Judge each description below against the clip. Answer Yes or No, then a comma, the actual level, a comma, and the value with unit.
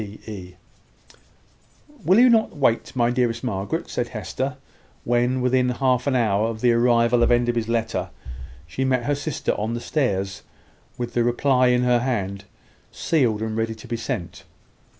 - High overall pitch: No, low, 120 Hz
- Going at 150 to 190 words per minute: Yes, average, 160 wpm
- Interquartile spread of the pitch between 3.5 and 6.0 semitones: No, narrow, 2.4 semitones